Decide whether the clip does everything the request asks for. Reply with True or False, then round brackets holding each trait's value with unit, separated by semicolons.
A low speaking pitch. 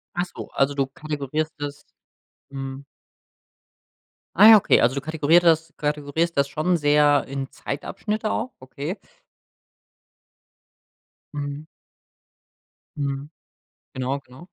False (145 Hz)